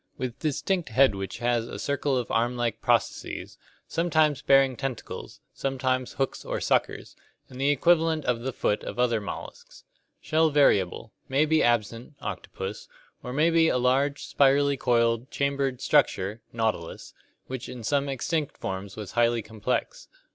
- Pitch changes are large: No, average, 3.6 semitones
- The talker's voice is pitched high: No, low, 130 Hz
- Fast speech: No, average, 150 wpm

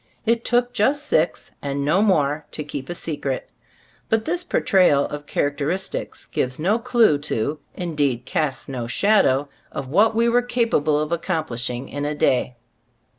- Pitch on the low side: No, medium, 155 Hz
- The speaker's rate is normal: Yes, average, 160 wpm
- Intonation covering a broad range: Yes, wide, 7.6 semitones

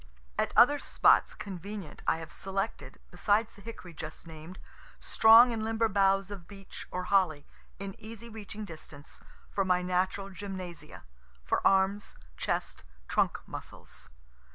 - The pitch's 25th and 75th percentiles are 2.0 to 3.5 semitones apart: Yes, average, 2.9 semitones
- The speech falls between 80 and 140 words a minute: Yes, slow, 135 wpm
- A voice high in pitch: Yes, high, 195 Hz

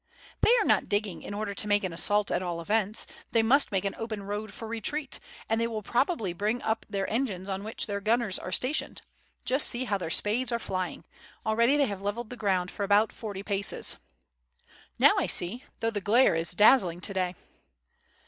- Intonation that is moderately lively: Yes, average, 3.0 semitones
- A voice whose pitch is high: Yes, high, 210 Hz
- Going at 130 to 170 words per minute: No, fast, 205 wpm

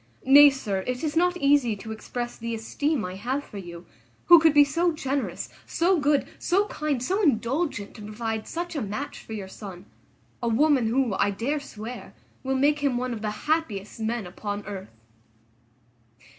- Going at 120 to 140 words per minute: No, average, 180 wpm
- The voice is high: Yes, very high, 250 Hz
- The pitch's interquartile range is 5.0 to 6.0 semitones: Yes, wide, 5.5 semitones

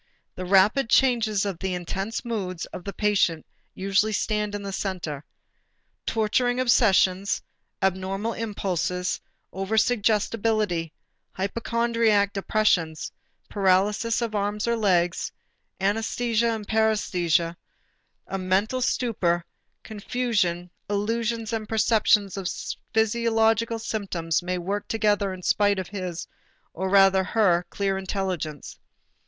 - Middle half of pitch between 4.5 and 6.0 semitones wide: No, average, 3.1 semitones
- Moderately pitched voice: No, high, 205 Hz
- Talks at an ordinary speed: No, slow, 110 wpm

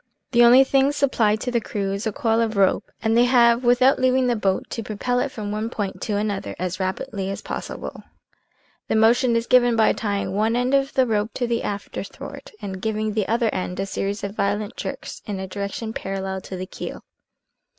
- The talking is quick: Yes, fast, 215 wpm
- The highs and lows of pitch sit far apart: No, average, 3.2 semitones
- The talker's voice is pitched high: Yes, high, 220 Hz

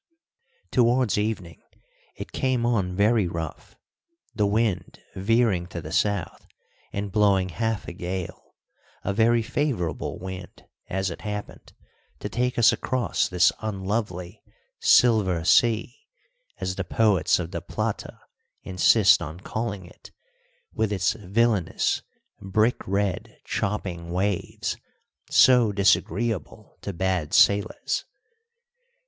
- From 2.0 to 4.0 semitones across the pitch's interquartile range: Yes, average, 3.6 semitones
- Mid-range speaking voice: No, low, 100 Hz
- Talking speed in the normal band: No, slow, 115 wpm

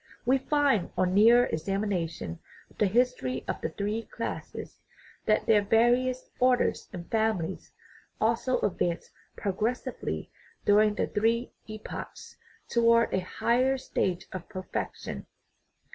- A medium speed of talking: No, slow, 115 wpm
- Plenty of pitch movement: No, average, 4.4 semitones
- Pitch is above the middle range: Yes, high, 215 Hz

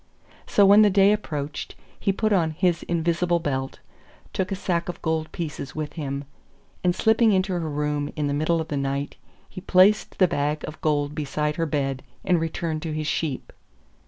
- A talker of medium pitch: Yes, medium, 160 Hz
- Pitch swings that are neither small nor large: Yes, average, 3.7 semitones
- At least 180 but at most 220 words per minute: Yes, average, 190 wpm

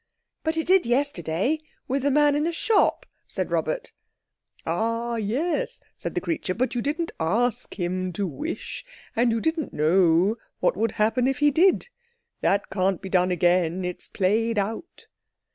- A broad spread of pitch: Yes, wide, 7.9 semitones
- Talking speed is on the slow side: No, average, 160 wpm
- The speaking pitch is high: Yes, high, 230 Hz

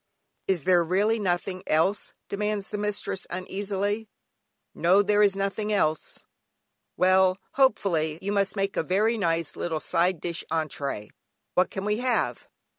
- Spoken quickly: No, average, 140 wpm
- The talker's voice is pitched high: Yes, high, 195 Hz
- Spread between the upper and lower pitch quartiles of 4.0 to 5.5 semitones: No, average, 3.0 semitones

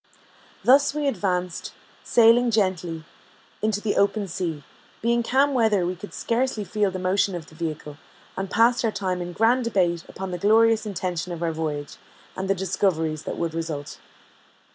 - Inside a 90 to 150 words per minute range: No, average, 165 wpm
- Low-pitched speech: No, high, 190 Hz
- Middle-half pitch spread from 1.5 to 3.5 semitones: No, average, 4.7 semitones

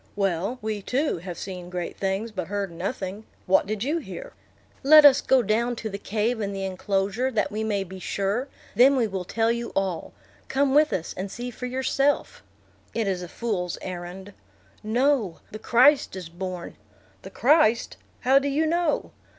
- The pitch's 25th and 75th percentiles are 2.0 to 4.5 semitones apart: No, average, 5.1 semitones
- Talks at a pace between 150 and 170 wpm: No, average, 180 wpm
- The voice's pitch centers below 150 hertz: No, high, 215 Hz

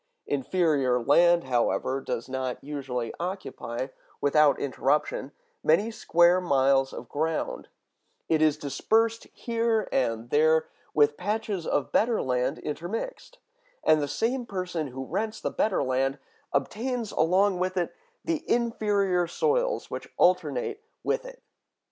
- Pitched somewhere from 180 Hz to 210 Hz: No, medium, 165 Hz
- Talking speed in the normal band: No, slow, 125 wpm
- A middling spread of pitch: No, wide, 7.9 semitones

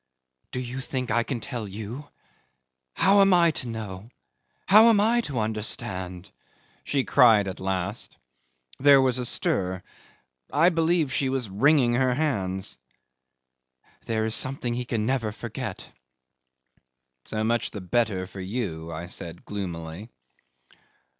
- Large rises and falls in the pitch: Yes, wide, 5.7 semitones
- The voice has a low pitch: Yes, low, 115 Hz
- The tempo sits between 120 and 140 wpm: Yes, slow, 135 wpm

